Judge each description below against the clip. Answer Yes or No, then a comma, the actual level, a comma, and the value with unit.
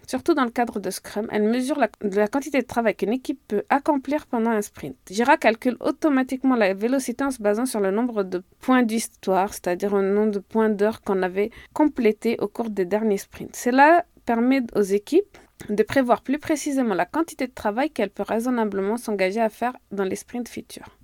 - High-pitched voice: Yes, high, 230 Hz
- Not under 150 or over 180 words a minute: No, average, 200 wpm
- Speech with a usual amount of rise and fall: Yes, average, 4.3 semitones